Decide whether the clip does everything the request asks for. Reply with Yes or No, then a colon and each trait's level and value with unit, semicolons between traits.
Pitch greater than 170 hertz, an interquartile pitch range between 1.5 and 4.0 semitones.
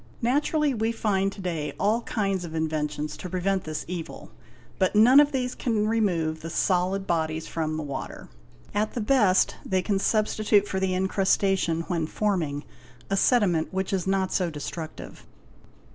No: high, 190 Hz; average, 4.4 semitones